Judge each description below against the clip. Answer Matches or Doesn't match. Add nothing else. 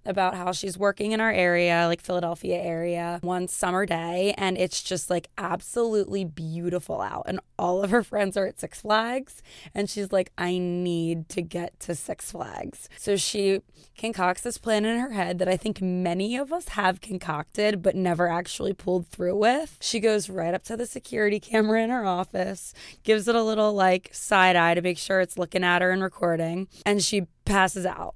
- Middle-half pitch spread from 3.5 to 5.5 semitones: Doesn't match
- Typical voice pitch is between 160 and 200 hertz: Matches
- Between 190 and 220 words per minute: Matches